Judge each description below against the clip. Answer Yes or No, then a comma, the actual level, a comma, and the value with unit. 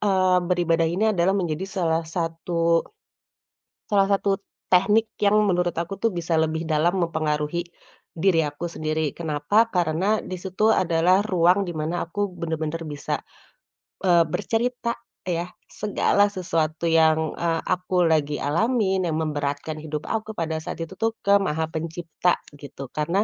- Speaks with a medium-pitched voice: Yes, medium, 170 Hz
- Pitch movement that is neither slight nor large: Yes, average, 3.3 semitones